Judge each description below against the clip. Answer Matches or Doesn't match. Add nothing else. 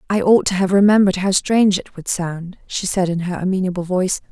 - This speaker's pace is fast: Matches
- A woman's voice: Matches